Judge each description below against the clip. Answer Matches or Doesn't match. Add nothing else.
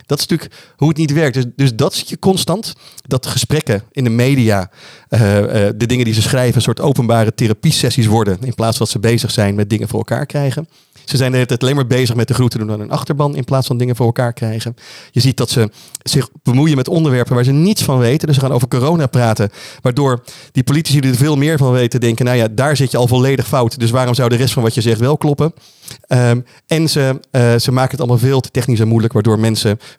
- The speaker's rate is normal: Doesn't match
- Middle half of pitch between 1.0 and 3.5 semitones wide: Matches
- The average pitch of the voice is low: Matches